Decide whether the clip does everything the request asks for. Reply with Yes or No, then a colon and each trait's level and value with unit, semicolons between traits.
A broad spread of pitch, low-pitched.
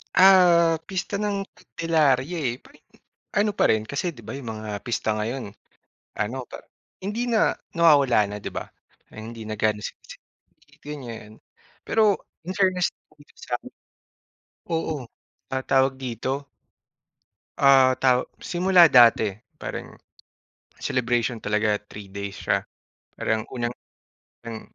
Yes: wide, 7.2 semitones; low, 130 Hz